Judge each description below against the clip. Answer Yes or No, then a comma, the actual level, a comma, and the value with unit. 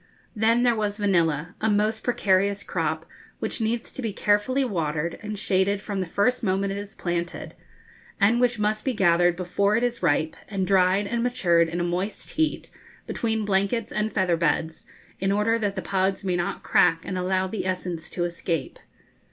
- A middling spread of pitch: Yes, average, 3.5 semitones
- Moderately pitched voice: No, high, 195 Hz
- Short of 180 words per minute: No, average, 185 wpm